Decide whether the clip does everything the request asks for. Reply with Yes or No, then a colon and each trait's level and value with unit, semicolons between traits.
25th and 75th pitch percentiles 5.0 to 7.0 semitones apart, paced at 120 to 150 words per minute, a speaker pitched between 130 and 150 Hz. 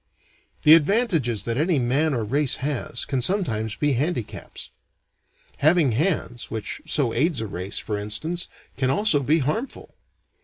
Yes: wide, 5.6 semitones; average, 145 wpm; medium, 140 Hz